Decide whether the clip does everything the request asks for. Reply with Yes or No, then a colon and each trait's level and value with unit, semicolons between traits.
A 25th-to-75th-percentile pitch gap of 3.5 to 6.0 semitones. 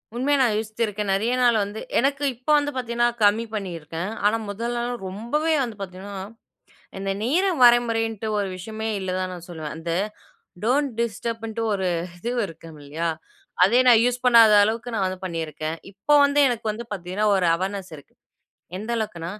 Yes: average, 4.2 semitones